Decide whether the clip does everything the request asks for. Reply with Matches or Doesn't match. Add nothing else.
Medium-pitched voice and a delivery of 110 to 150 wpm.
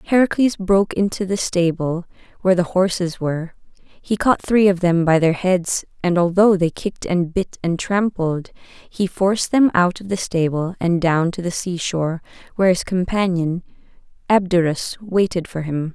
Doesn't match